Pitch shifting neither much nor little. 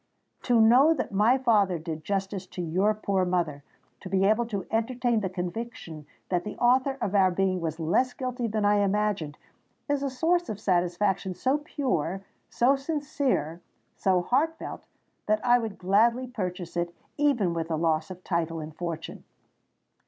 No: wide, 5.7 semitones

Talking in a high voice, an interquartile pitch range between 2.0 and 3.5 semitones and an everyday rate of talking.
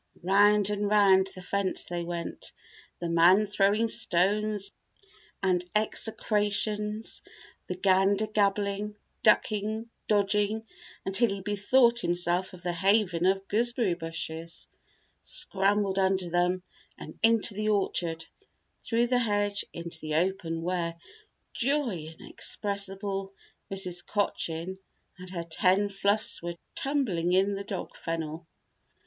No: high, 195 Hz; average, 3.0 semitones; slow, 115 wpm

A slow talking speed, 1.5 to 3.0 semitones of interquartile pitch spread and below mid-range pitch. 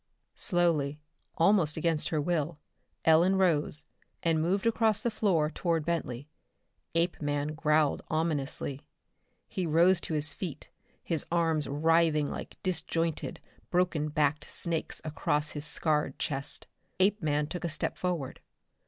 No: slow, 125 wpm; narrow, 2.6 semitones; medium, 160 Hz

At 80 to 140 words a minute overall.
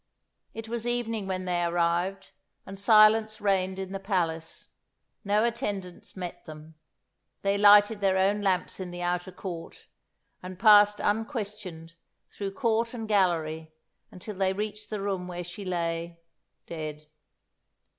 Yes: slow, 135 wpm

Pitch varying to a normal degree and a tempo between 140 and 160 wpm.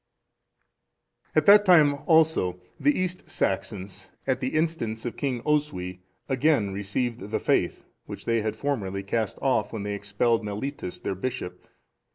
No: wide, 6.4 semitones; average, 150 wpm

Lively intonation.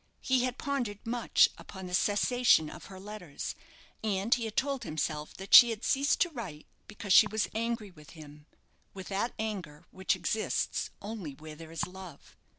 Yes: wide, 5.7 semitones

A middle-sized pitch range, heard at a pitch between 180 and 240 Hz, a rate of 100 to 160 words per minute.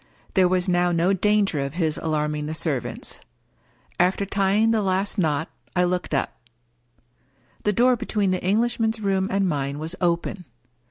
Yes: average, 3.9 semitones; medium, 185 Hz; average, 155 wpm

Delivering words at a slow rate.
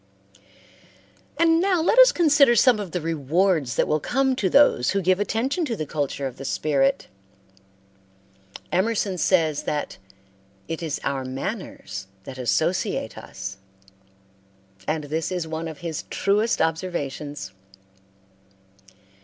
Yes: slow, 130 wpm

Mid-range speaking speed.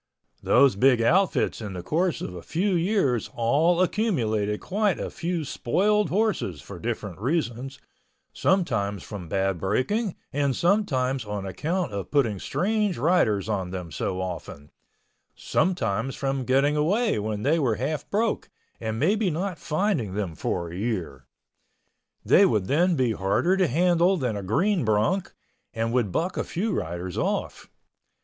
Yes: average, 150 wpm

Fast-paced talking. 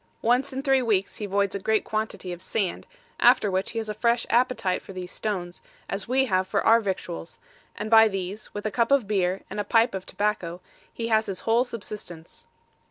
Yes: fast, 210 wpm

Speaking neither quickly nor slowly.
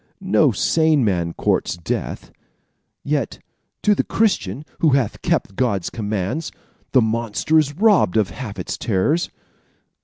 No: slow, 130 wpm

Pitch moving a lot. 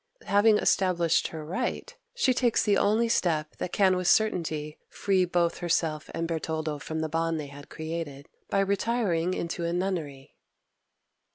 No: average, 3.7 semitones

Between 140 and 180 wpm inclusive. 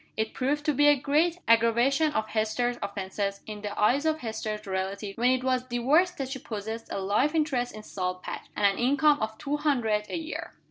No: fast, 205 wpm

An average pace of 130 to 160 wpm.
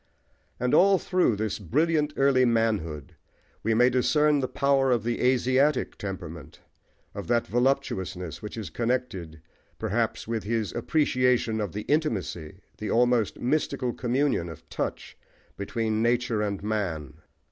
Yes: slow, 135 wpm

